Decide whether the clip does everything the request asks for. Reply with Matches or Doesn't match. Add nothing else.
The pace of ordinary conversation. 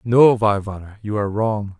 Matches